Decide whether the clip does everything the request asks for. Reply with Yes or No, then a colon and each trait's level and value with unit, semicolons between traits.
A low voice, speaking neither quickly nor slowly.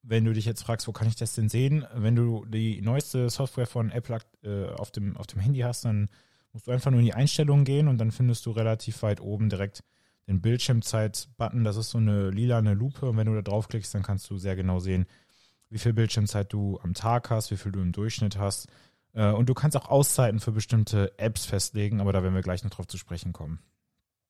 No: low, 110 Hz; fast, 230 wpm